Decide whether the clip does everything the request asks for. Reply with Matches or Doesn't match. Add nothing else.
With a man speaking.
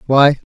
Matches